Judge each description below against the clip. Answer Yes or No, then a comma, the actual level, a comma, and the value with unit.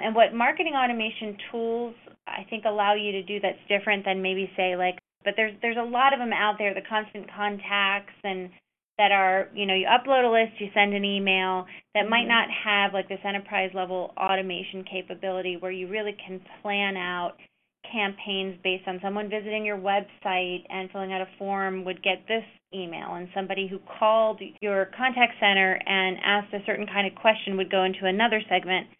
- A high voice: Yes, high, 200 Hz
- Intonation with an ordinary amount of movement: No, narrow, 2.1 semitones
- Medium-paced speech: Yes, average, 190 wpm